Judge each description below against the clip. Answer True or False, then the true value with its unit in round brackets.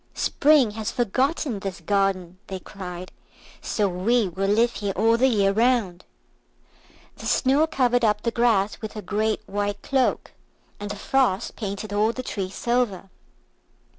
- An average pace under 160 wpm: True (150 wpm)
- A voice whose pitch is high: True (210 Hz)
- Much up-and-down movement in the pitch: False (3.6 semitones)